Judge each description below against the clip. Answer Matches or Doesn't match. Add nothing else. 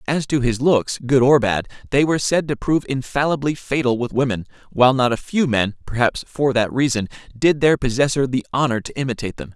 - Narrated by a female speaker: Doesn't match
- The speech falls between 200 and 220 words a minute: Matches